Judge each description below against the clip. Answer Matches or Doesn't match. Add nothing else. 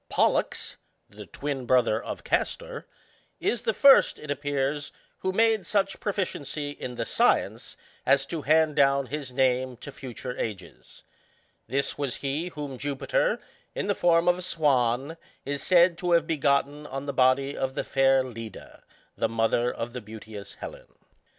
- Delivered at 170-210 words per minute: Doesn't match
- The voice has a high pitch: Doesn't match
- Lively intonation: Doesn't match